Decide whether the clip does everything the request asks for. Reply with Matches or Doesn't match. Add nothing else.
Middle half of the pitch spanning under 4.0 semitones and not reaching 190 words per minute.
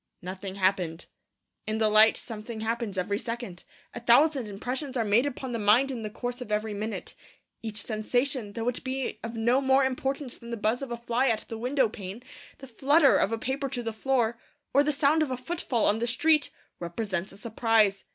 Doesn't match